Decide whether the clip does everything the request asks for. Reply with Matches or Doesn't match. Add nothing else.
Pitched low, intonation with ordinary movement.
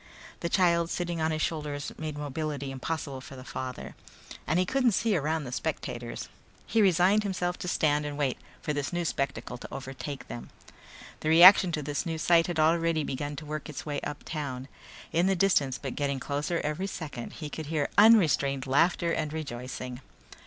Doesn't match